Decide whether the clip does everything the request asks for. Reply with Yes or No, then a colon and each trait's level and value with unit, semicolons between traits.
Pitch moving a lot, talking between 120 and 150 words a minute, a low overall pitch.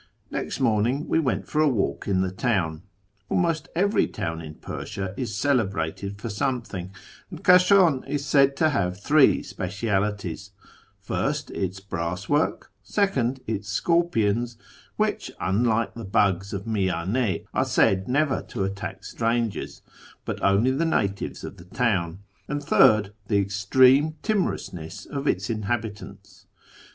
Yes: wide, 5.7 semitones; average, 140 wpm; low, 110 Hz